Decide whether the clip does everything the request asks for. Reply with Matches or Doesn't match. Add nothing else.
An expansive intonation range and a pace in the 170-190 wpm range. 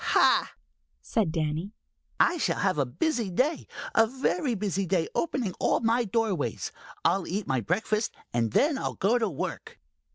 Doesn't match